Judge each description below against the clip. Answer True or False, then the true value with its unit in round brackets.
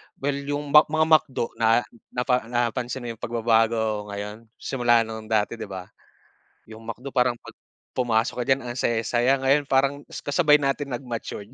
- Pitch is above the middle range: False (120 Hz)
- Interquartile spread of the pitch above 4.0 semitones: False (3.4 semitones)